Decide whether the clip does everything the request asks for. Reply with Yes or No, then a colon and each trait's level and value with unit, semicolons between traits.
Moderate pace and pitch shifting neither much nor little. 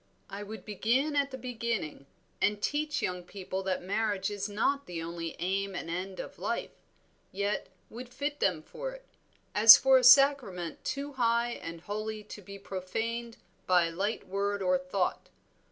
Yes: average, 170 wpm; average, 4.6 semitones